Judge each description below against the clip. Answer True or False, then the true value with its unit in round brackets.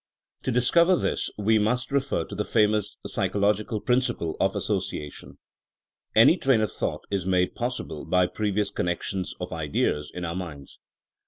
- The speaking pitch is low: True (105 Hz)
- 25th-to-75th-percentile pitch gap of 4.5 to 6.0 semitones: True (4.8 semitones)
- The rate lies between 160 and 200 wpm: False (150 wpm)